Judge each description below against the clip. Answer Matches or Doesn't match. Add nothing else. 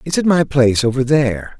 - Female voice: Doesn't match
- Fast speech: Matches